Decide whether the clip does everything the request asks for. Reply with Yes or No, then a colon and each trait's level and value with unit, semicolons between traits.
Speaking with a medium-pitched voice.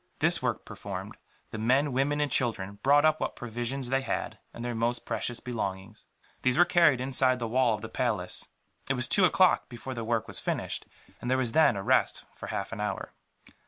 No: low, 125 Hz